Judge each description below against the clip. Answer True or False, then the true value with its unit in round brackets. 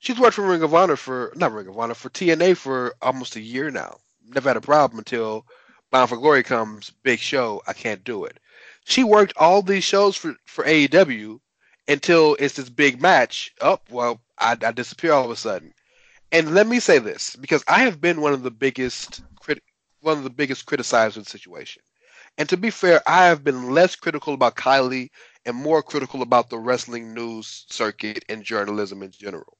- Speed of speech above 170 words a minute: True (205 wpm)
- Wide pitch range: True (6.2 semitones)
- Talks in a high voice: False (140 Hz)